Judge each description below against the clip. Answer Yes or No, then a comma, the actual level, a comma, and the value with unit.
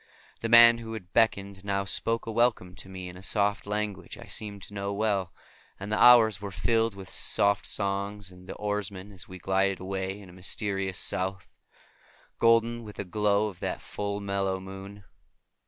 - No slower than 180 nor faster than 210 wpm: Yes, average, 185 wpm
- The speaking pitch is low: Yes, low, 100 Hz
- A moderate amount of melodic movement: No, narrow, 1.8 semitones